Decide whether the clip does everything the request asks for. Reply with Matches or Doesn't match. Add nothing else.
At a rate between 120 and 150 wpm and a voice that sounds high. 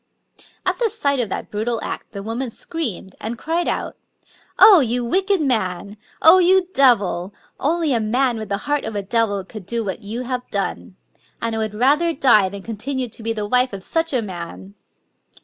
Doesn't match